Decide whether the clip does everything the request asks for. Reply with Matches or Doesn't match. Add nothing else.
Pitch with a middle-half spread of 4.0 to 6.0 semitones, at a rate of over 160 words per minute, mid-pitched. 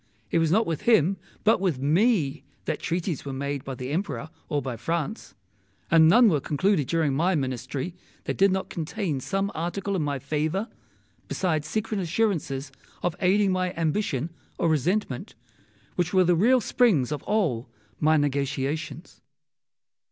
Doesn't match